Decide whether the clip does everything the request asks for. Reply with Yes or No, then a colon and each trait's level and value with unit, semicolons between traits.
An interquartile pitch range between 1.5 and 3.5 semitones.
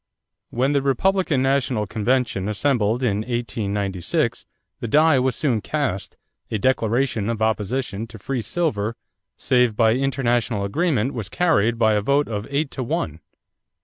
No: average, 4.3 semitones